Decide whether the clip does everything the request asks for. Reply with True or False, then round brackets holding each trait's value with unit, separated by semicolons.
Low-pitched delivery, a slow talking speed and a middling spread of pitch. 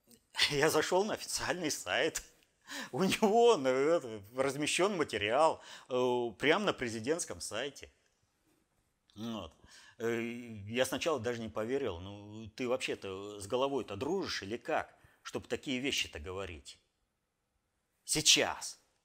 True (120 Hz; 105 wpm; 3.9 semitones)